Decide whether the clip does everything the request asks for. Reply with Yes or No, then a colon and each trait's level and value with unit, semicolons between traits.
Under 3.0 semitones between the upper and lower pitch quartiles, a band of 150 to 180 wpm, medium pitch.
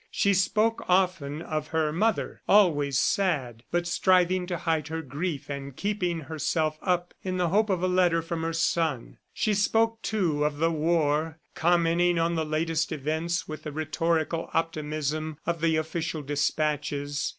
Yes: narrow, 2.6 semitones; average, 160 wpm; medium, 165 Hz